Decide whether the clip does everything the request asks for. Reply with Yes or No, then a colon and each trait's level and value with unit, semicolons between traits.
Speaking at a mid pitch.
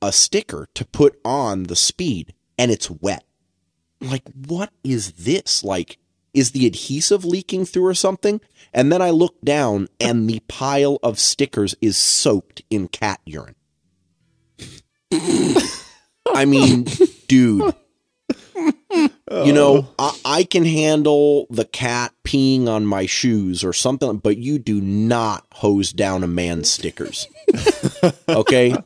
No: low, 125 Hz